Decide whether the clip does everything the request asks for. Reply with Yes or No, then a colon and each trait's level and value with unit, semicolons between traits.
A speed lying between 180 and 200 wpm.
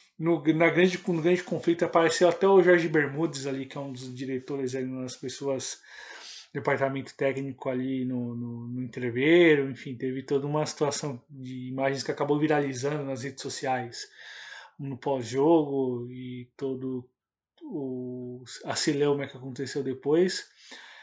No: average, 140 wpm